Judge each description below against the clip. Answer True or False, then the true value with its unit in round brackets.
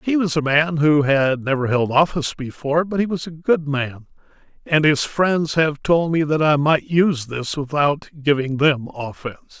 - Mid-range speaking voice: True (150 Hz)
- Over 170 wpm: True (195 wpm)